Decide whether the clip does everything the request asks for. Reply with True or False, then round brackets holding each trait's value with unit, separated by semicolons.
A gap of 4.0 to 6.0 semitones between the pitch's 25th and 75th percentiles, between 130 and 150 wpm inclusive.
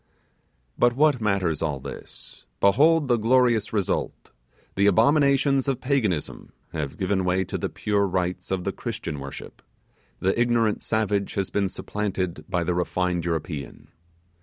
True (5.0 semitones; 140 wpm)